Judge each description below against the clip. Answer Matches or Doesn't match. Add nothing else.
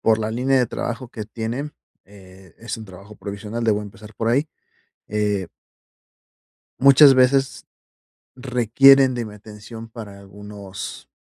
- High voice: Doesn't match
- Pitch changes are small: Doesn't match